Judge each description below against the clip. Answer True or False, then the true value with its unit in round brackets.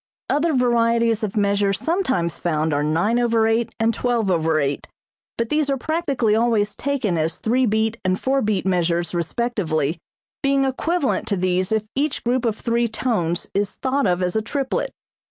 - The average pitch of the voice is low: False (220 Hz)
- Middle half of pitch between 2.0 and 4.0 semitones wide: False (5.6 semitones)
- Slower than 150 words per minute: False (155 wpm)